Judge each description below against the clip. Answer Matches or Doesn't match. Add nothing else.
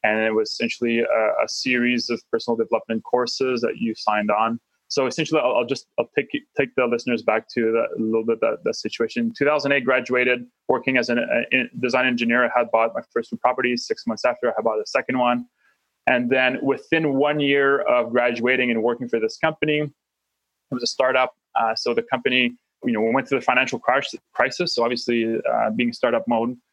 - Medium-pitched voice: Doesn't match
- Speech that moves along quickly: Matches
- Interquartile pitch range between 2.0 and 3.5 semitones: Matches